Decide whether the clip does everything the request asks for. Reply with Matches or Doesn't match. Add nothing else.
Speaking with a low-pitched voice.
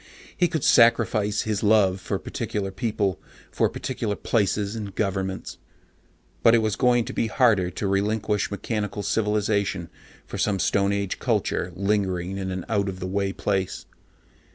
Matches